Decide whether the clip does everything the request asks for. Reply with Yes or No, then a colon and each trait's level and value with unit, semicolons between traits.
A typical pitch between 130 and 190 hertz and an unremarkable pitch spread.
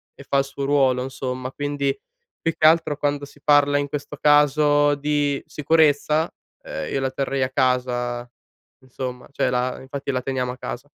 No: medium, 140 Hz; narrow, 2.1 semitones